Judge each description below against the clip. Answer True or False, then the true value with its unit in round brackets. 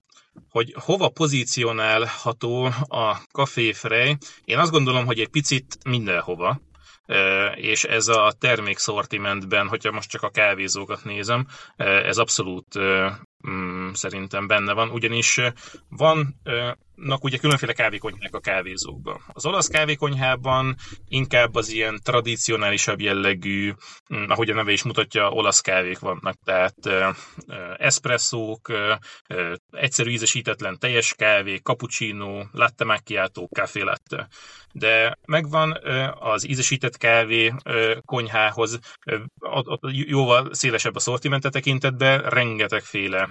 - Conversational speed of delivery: False (100 wpm)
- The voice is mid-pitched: False (115 Hz)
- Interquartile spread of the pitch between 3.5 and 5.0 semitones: True (4.1 semitones)